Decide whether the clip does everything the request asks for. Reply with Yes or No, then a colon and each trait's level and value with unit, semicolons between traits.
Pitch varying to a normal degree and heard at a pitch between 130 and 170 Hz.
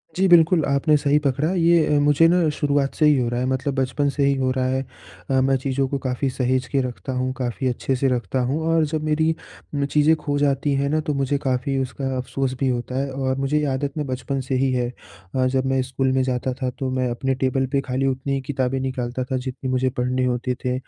No: narrow, 1.8 semitones; low, 135 Hz